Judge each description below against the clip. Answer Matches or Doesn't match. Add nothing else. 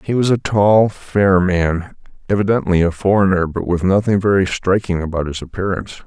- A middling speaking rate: Matches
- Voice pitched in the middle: Doesn't match